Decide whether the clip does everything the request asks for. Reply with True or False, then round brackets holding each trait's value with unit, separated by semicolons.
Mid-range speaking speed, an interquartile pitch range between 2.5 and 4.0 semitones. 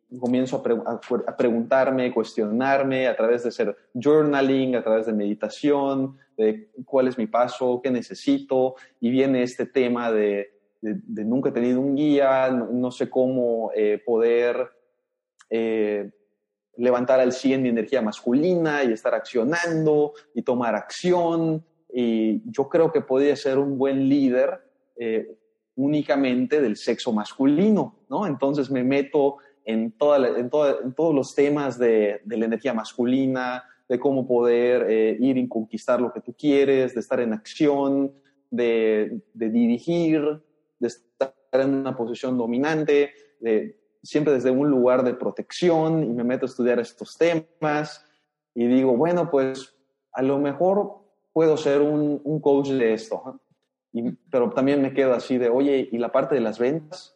True (165 wpm; 3.4 semitones)